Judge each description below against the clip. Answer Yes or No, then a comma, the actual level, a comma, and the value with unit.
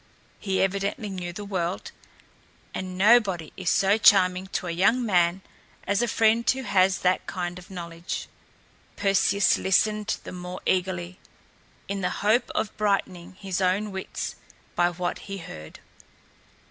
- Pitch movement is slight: Yes, narrow, 2.3 semitones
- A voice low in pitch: No, high, 190 Hz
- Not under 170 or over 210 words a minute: No, average, 145 wpm